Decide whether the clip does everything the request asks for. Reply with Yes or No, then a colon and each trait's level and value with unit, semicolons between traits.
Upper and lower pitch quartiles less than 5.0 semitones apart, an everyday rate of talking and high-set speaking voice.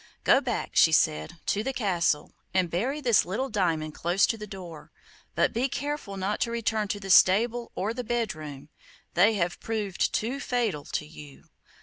No: average, 5.3 semitones; average, 185 wpm; high, 205 Hz